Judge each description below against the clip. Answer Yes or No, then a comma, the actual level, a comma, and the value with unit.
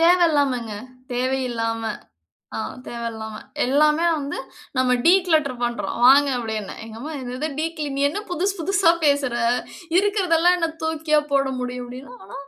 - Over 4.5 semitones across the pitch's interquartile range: Yes, average, 5.0 semitones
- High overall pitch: Yes, very high, 280 Hz